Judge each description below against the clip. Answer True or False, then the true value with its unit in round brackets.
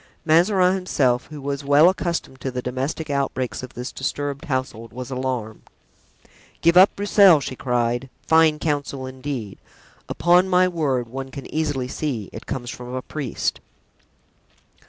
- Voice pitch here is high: False (140 Hz)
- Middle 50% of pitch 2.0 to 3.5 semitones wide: False (4.0 semitones)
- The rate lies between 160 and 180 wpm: False (145 wpm)